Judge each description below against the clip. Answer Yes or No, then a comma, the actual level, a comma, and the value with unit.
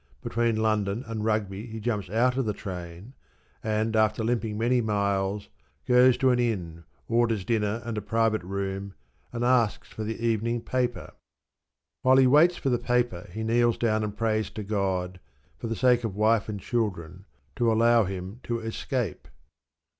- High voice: No, low, 110 Hz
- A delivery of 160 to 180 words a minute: Yes, average, 170 wpm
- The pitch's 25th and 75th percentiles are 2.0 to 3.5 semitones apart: Yes, average, 2.7 semitones